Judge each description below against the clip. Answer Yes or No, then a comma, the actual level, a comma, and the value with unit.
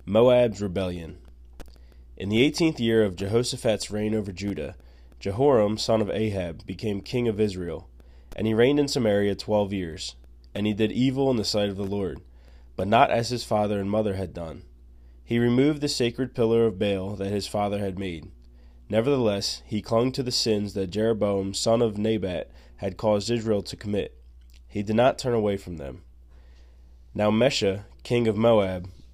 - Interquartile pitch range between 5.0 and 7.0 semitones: Yes, average, 5.3 semitones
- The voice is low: Yes, low, 100 Hz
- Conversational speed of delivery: Yes, average, 175 wpm